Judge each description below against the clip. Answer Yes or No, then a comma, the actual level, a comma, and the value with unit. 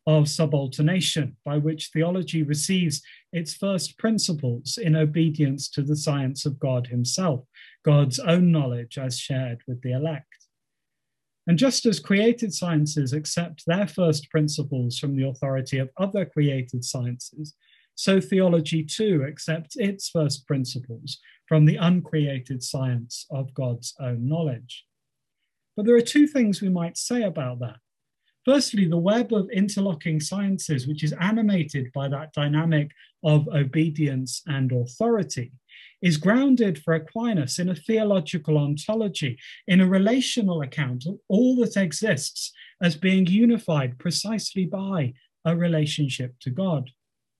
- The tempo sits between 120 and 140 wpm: Yes, slow, 135 wpm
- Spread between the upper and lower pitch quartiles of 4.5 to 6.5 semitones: Yes, wide, 5.5 semitones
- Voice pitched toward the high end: No, medium, 155 Hz